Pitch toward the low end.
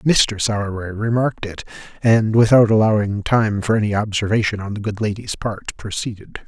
Yes: low, 105 Hz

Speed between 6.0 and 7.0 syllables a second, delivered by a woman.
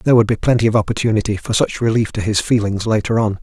No: 6.8 syllables/s; male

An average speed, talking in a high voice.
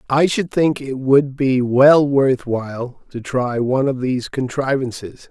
No: average, 170 wpm; low, 135 Hz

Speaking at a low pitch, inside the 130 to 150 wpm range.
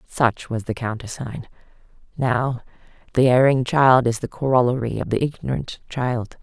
Yes: low, 125 Hz; average, 140 wpm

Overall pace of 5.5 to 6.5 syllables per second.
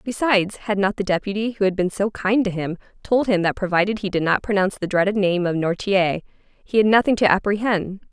Yes: 5.7 syllables/s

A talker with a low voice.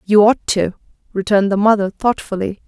No: high, 200 Hz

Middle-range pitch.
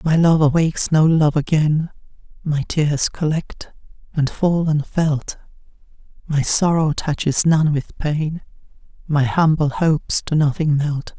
Yes: medium, 155 Hz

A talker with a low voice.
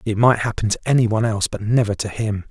Yes: low, 110 Hz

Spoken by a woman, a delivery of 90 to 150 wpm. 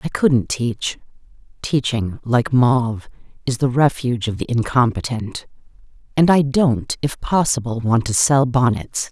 Yes: female; average, 140 wpm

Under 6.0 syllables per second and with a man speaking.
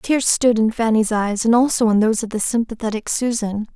No: 5.5 syllables/s; female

